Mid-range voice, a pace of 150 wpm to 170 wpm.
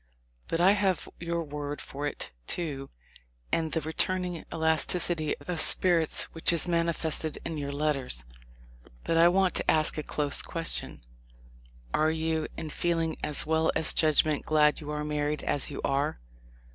Yes: medium, 160 Hz; average, 155 wpm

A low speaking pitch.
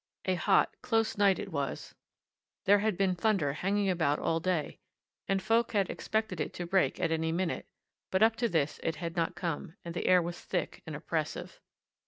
No: medium, 185 Hz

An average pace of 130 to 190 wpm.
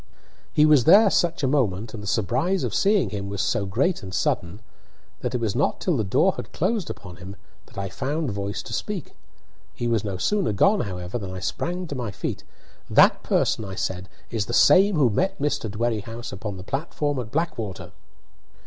No: average, 200 wpm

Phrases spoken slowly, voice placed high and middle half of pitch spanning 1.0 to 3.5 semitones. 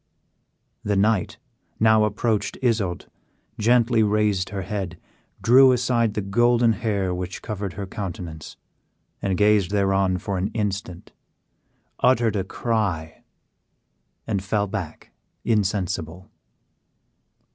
No: slow, 105 wpm; low, 105 Hz; average, 2.9 semitones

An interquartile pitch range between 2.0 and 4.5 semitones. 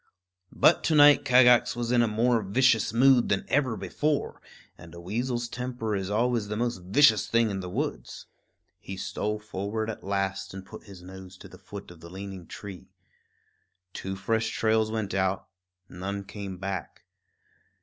Yes: average, 3.6 semitones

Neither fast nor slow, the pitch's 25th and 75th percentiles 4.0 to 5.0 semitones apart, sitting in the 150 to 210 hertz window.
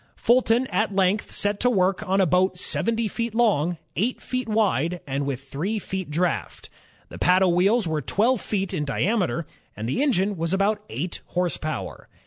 Yes: average, 175 wpm; average, 4.5 semitones; high, 190 Hz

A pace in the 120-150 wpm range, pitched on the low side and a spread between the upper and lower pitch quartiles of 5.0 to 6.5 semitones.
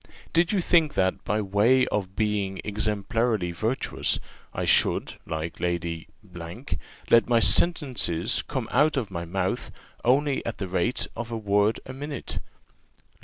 Yes: average, 145 wpm; low, 110 Hz; wide, 5.6 semitones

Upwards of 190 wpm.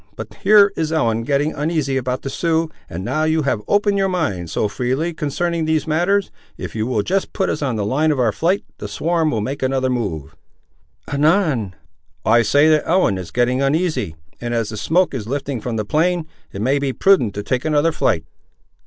Yes: fast, 205 wpm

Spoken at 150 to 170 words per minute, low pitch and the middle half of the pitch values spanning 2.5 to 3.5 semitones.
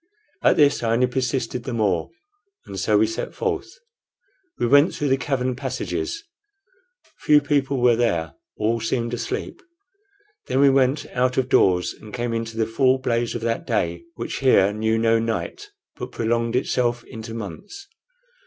Yes: average, 160 wpm; low, 120 Hz; average, 2.8 semitones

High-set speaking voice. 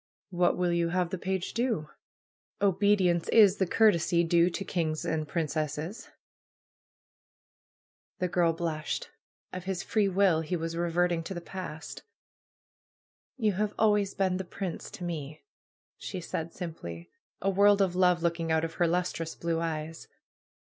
No: medium, 175 Hz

